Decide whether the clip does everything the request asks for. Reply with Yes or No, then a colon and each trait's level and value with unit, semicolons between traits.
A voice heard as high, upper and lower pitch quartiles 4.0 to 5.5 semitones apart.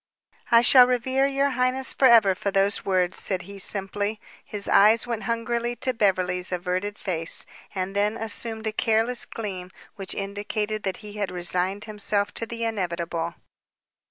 No: high, 205 Hz; average, 3.3 semitones